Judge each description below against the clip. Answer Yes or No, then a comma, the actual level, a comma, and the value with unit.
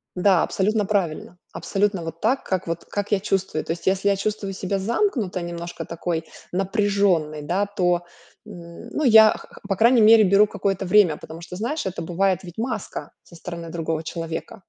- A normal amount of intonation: Yes, average, 3.2 semitones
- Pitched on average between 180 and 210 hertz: Yes, high, 190 Hz